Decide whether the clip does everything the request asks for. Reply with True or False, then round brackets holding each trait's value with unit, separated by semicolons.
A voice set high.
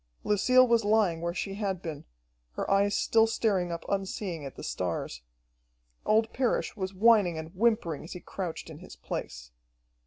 True (195 Hz)